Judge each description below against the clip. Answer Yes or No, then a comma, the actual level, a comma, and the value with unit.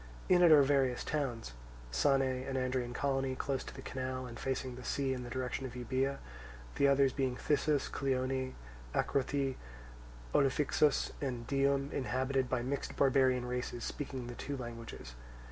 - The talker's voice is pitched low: Yes, low, 130 Hz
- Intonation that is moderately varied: No, narrow, 1.5 semitones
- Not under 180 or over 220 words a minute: No, average, 155 wpm